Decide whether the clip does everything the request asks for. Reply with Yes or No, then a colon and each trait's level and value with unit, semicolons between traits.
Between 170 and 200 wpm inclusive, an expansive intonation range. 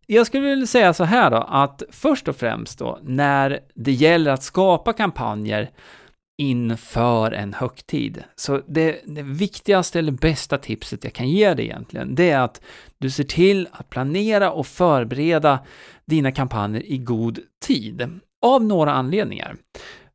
No: average, 150 wpm; wide, 6.0 semitones